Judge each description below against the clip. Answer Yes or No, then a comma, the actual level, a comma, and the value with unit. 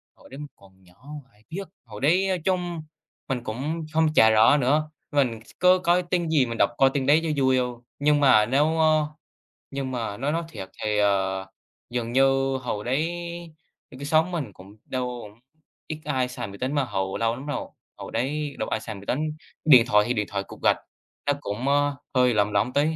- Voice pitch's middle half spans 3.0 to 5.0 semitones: No, wide, 5.5 semitones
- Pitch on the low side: Yes, low, 130 Hz